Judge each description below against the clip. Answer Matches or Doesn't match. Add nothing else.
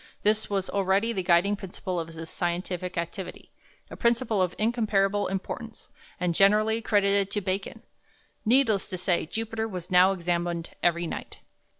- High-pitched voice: Matches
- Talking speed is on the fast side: Doesn't match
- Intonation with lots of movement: Doesn't match